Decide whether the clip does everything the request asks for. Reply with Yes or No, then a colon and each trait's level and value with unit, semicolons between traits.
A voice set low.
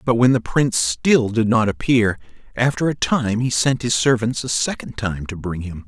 Yes: low, 115 Hz